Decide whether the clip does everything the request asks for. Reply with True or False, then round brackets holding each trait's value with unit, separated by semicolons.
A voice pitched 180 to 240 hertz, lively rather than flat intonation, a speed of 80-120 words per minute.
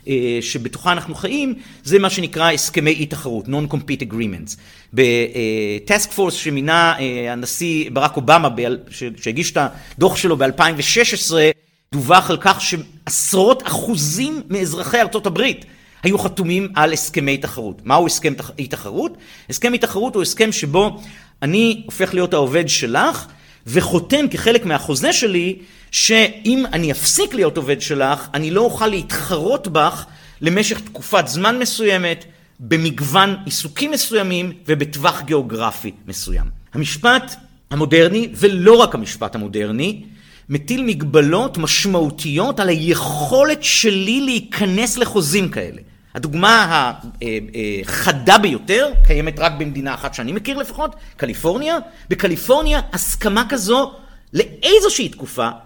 False (170 Hz; 6.9 semitones; 110 wpm)